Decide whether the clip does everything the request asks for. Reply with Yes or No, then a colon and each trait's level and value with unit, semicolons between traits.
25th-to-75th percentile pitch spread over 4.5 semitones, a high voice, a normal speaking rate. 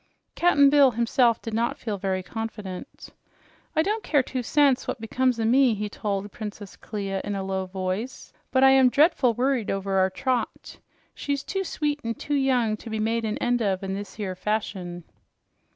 Yes: average, 4.9 semitones; high, 225 Hz; average, 180 wpm